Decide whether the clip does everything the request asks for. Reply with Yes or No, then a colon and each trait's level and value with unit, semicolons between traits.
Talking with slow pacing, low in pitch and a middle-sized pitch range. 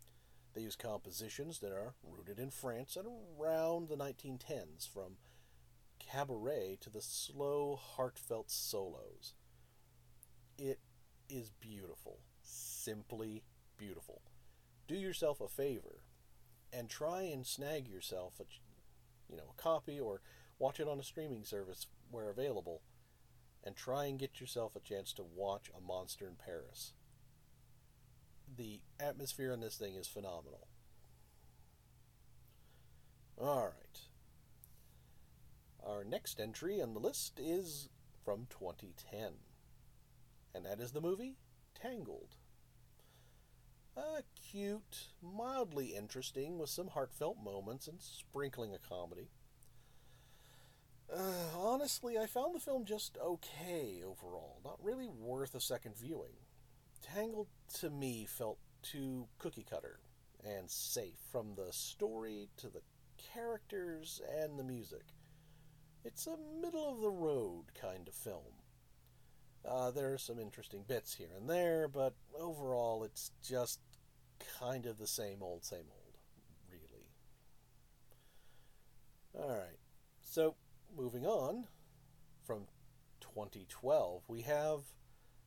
No: slow, 120 wpm; low, 130 Hz; wide, 6.0 semitones